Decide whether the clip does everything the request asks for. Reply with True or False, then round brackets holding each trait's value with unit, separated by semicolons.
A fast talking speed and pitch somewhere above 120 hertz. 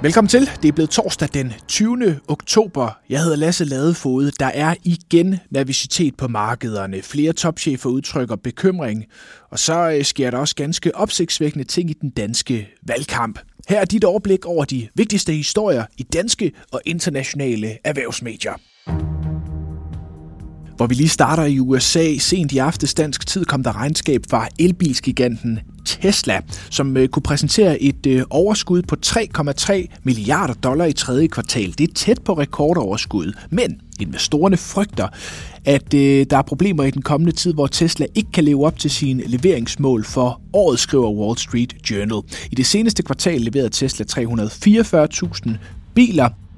False (150 wpm; 140 Hz)